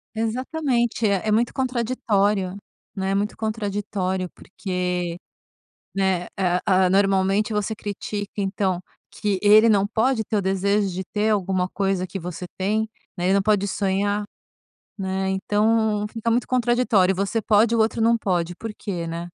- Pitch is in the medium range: No, high, 200 Hz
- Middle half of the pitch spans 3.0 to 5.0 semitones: No, narrow, 2.5 semitones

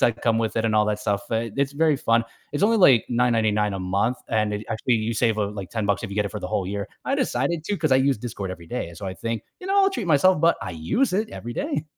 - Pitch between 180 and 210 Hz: No, low, 115 Hz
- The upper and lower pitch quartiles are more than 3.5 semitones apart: Yes, average, 5.3 semitones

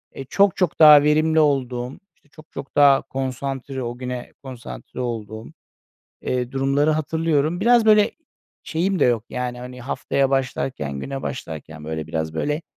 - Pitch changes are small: No, average, 3.7 semitones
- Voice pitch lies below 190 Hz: Yes, low, 135 Hz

